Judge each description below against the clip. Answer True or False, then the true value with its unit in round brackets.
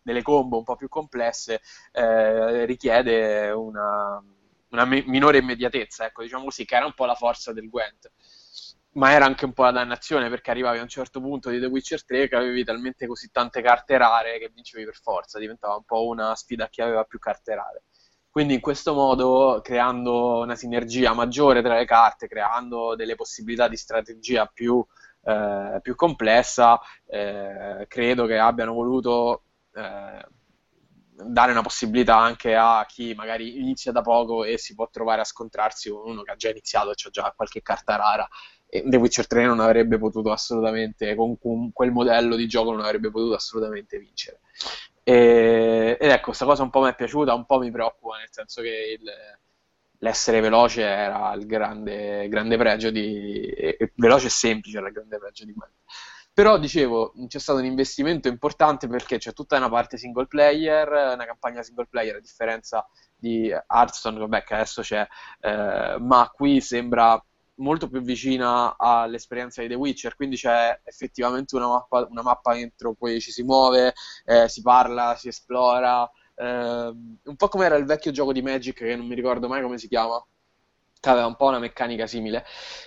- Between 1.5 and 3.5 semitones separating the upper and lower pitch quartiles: True (2.6 semitones)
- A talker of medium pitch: False (120 Hz)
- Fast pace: True (180 wpm)